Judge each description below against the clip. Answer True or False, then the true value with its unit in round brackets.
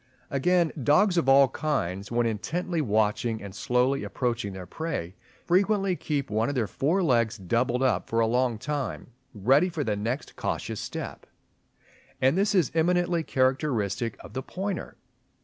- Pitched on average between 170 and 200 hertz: False (130 Hz)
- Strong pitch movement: True (6.3 semitones)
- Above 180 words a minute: False (155 wpm)